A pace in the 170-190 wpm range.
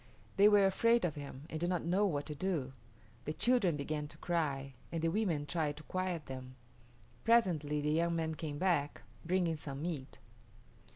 Yes: average, 180 wpm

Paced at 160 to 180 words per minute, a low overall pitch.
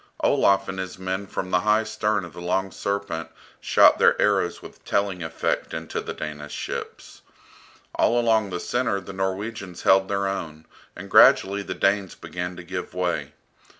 Yes: average, 170 wpm; very low, 95 Hz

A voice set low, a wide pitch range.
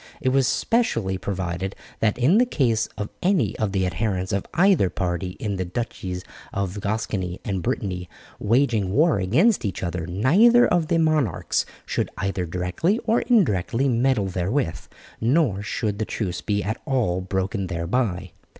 Yes: low, 105 Hz; wide, 6.1 semitones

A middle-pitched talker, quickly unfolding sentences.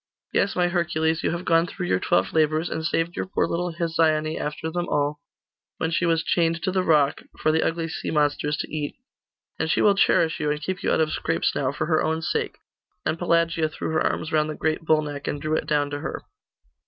Yes: medium, 160 Hz; fast, 230 wpm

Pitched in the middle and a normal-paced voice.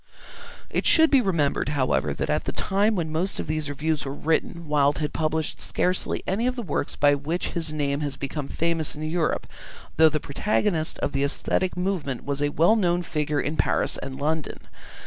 Yes: medium, 155 Hz; average, 195 wpm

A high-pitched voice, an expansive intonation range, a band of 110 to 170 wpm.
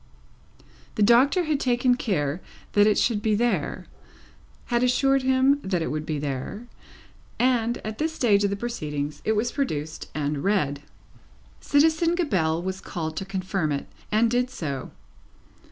Yes: high, 210 Hz; wide, 7.9 semitones; average, 155 wpm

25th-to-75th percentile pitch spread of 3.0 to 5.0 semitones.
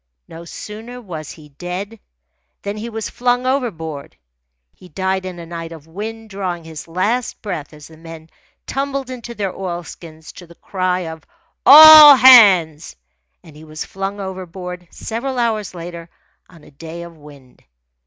No: wide, 5.4 semitones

